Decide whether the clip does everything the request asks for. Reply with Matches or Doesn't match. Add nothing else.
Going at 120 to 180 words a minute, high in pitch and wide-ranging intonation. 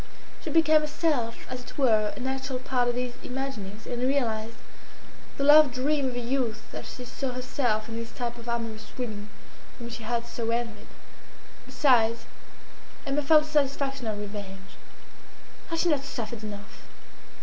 Doesn't match